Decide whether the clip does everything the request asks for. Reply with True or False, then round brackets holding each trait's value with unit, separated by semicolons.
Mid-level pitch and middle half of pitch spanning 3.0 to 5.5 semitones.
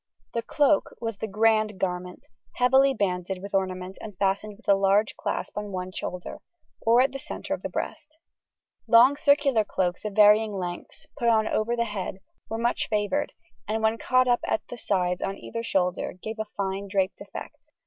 False (210 Hz; 3.4 semitones)